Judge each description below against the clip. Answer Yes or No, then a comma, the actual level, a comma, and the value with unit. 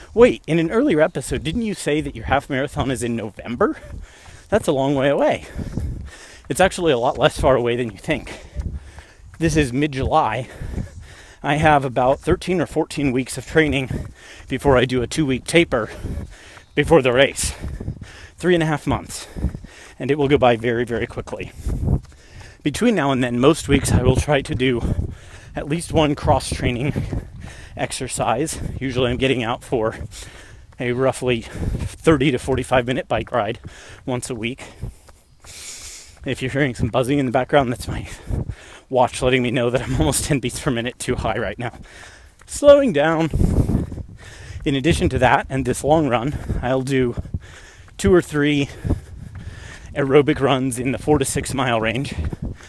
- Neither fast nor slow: Yes, average, 170 wpm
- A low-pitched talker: Yes, low, 130 Hz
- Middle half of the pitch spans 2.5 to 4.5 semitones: No, average, 5.2 semitones